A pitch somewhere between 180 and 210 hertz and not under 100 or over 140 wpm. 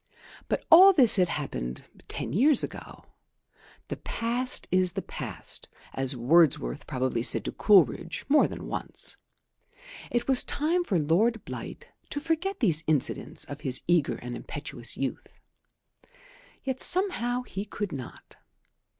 Yes: medium, 185 Hz; slow, 135 wpm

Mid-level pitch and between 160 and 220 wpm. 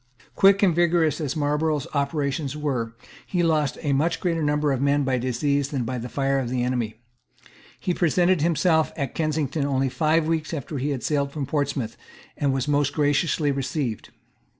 Yes: medium, 145 Hz; average, 175 wpm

